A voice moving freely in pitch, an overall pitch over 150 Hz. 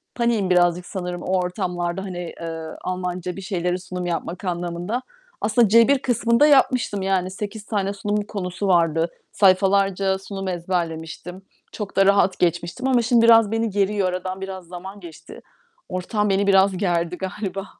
No: narrow, 2.4 semitones; high, 190 Hz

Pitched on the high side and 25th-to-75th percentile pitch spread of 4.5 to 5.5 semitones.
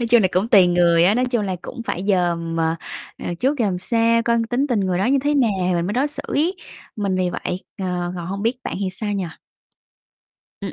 Yes: high, 200 Hz; average, 4.8 semitones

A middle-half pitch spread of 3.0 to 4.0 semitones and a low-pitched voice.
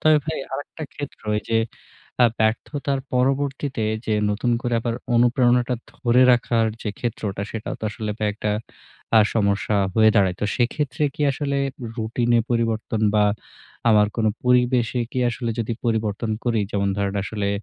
No: narrow, 2.5 semitones; low, 115 Hz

